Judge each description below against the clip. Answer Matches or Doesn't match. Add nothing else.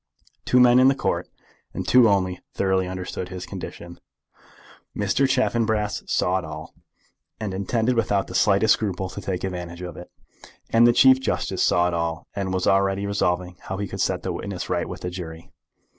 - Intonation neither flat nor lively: Matches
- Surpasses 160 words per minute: Matches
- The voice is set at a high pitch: Doesn't match